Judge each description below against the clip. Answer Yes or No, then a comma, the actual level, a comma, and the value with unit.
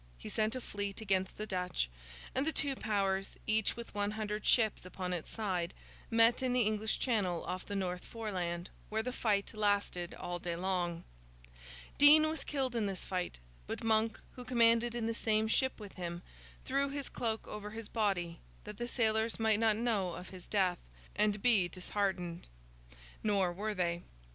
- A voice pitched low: No, high, 210 Hz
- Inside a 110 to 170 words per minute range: No, average, 180 wpm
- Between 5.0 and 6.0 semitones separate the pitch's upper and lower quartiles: No, average, 3.7 semitones